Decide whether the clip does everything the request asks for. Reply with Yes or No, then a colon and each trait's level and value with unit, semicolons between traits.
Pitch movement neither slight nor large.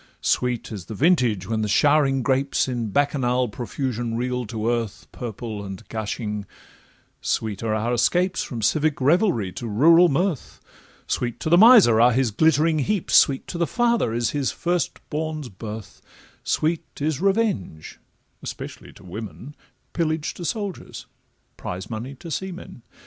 No: wide, 6.2 semitones